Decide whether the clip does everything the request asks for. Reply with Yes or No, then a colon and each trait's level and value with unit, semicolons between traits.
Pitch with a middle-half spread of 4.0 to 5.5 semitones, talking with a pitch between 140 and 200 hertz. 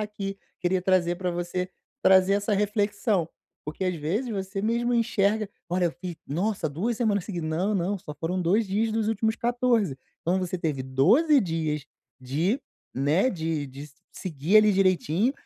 Yes: average, 4.4 semitones; high, 190 Hz